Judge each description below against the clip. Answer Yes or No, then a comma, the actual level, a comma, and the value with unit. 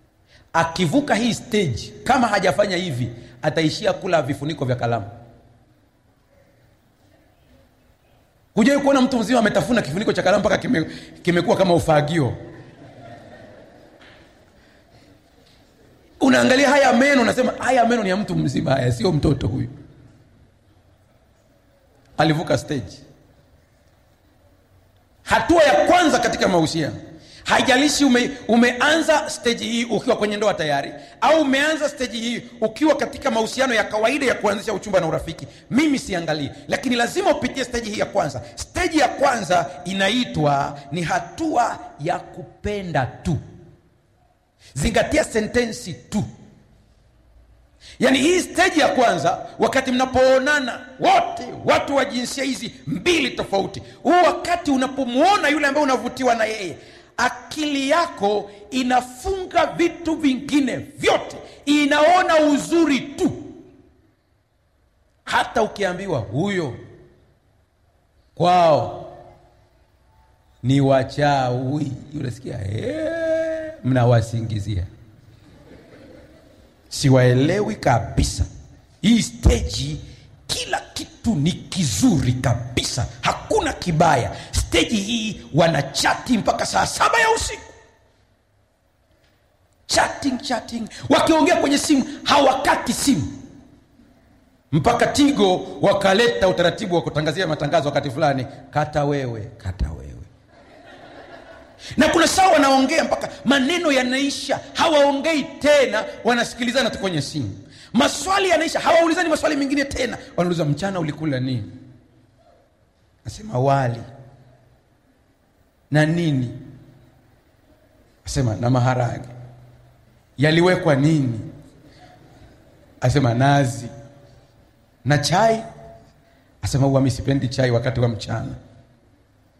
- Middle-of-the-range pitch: Yes, medium, 175 Hz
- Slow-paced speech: Yes, slow, 95 wpm